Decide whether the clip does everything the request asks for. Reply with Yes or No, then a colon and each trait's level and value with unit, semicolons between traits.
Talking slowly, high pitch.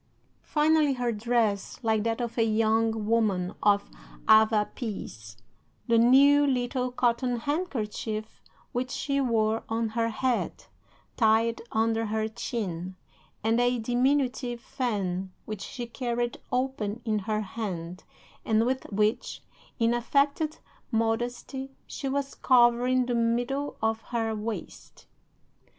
Yes: slow, 120 wpm; high, 230 Hz